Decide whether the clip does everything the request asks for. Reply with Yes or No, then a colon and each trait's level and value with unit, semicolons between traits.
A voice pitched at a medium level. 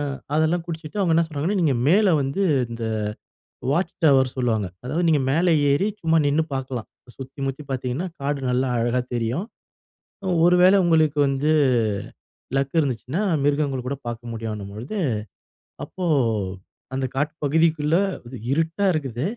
Yes: medium, 145 Hz